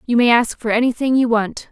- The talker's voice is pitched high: Yes, high, 235 Hz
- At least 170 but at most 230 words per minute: No, fast, 245 wpm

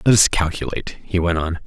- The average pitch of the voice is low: Yes, very low, 90 Hz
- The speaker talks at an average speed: No, fast, 215 wpm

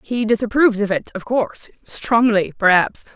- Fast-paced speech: No, slow, 135 wpm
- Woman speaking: Yes, female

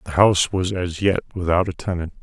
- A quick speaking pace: Yes, fast, 215 wpm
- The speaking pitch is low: Yes, very low, 90 Hz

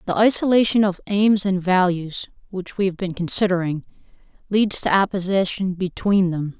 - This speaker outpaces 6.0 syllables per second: No, 4.9 syllables/s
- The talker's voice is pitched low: No, high, 190 Hz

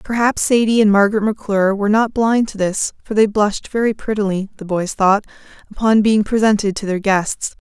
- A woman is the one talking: Yes, female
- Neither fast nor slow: Yes, average, 190 wpm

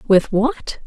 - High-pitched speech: Yes, high, 235 Hz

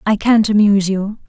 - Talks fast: No, average, 190 wpm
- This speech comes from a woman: Yes, female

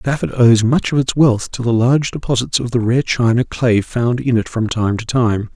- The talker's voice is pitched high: No, low, 120 Hz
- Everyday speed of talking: No, fast, 240 wpm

